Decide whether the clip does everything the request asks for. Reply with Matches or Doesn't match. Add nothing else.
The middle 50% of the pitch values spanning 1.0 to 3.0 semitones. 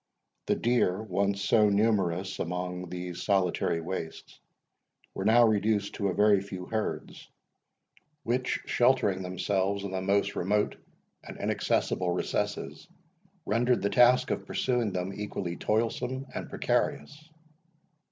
Doesn't match